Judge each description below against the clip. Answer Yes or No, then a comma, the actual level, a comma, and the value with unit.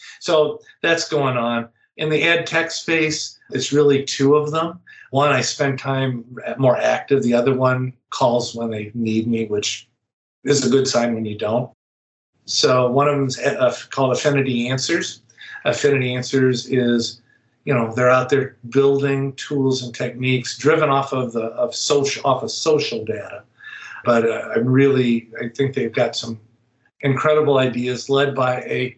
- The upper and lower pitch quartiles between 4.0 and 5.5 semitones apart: No, average, 2.9 semitones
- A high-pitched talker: No, low, 130 Hz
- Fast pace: No, average, 165 wpm